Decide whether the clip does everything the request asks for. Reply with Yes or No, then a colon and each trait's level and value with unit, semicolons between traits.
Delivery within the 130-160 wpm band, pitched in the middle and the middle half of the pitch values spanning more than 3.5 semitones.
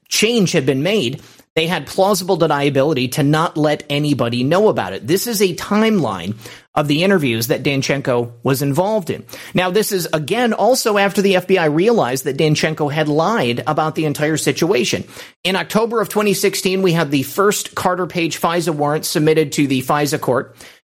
No: average, 175 wpm; medium, 160 Hz; average, 4.8 semitones